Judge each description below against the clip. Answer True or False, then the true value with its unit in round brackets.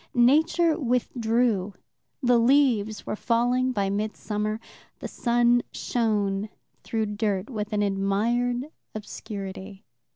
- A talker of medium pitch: False (225 Hz)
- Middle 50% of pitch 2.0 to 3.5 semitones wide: True (3.0 semitones)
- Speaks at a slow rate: True (100 wpm)